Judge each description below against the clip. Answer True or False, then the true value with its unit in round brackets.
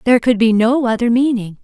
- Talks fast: True (220 wpm)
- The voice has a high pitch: True (235 Hz)